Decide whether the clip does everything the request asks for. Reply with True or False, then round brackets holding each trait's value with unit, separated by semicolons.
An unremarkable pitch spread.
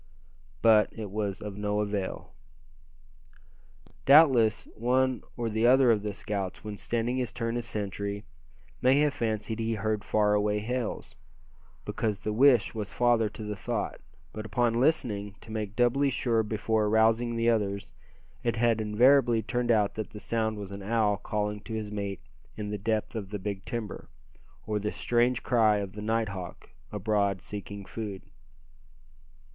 False (2.2 semitones)